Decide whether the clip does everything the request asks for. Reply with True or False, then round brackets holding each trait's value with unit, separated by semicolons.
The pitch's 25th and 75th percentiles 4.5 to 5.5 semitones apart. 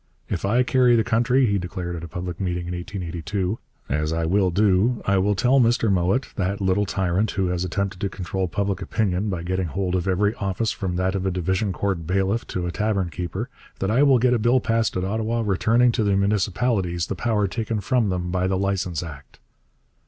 False (3.4 semitones)